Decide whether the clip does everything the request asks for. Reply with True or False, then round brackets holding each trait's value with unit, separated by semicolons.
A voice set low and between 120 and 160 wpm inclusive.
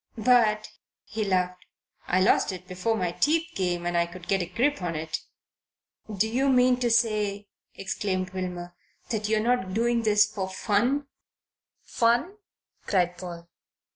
False (205 Hz; 150 wpm)